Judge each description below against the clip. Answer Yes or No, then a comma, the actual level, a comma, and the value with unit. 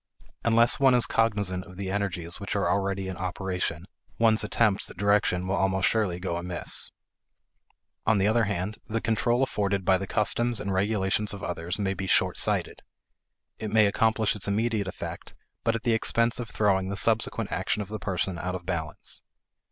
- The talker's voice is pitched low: Yes, low, 100 Hz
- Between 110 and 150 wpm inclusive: No, average, 185 wpm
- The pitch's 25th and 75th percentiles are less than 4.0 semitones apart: Yes, average, 2.9 semitones